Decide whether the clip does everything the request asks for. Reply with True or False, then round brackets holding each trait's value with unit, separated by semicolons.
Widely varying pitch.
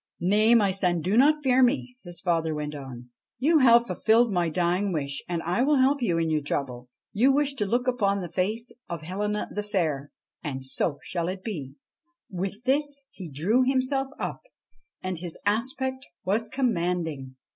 True (7.0 semitones)